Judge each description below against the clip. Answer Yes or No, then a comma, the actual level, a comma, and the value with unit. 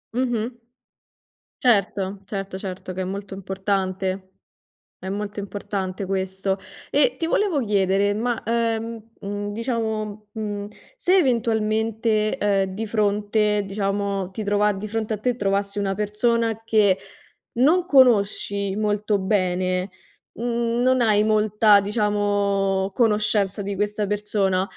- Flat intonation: Yes, narrow, 2.2 semitones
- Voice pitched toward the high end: Yes, high, 205 Hz